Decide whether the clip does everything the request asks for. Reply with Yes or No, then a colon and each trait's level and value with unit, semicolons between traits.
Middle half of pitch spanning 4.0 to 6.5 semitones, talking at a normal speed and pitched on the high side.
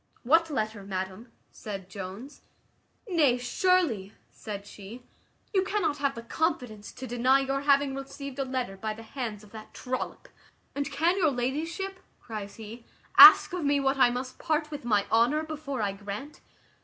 Yes: average, 5.1 semitones; average, 165 wpm; very high, 255 Hz